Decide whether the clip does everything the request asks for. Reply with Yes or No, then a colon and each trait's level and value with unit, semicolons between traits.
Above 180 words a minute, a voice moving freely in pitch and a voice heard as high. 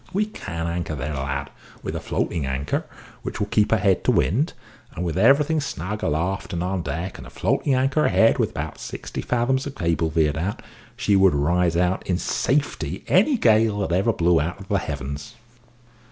No: average, 195 wpm; wide, 5.9 semitones; very low, 90 Hz